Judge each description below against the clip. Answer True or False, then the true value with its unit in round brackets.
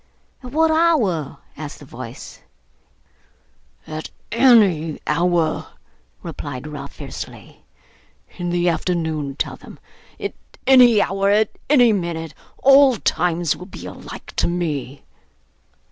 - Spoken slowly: True (115 wpm)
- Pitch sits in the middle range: True (175 Hz)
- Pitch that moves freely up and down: True (6.9 semitones)